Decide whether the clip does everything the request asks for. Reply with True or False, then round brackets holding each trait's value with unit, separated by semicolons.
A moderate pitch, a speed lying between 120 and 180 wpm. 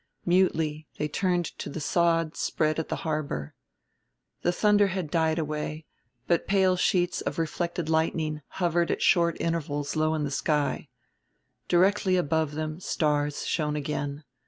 True (160 Hz; 145 wpm)